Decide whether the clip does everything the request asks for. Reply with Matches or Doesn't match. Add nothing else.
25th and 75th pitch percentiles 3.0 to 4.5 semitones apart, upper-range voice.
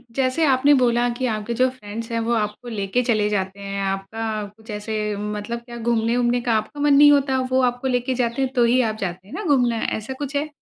Matches